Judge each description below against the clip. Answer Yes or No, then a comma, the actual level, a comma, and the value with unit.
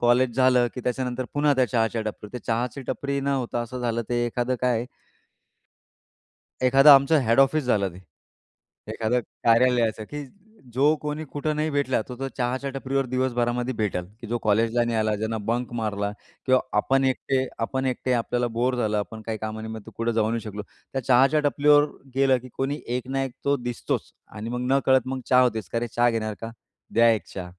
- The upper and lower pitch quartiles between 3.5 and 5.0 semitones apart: No, average, 2.8 semitones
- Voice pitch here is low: Yes, low, 125 Hz